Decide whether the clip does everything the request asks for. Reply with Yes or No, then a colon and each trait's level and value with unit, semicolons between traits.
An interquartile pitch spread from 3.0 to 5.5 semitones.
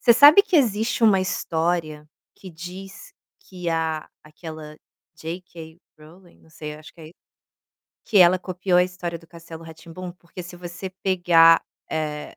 No: narrow, 2.4 semitones